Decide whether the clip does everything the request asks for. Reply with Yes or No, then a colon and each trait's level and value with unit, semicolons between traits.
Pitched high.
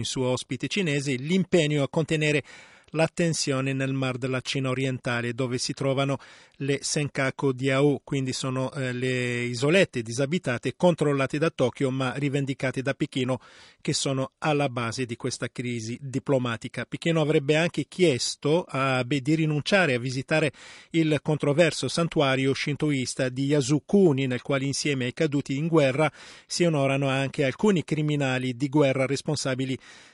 No: medium, 140 Hz